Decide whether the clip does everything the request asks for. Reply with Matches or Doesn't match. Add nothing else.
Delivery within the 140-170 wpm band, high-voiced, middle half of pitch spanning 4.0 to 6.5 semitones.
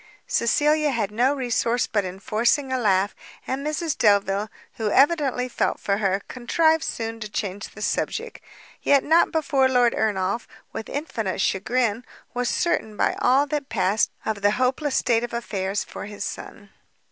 Matches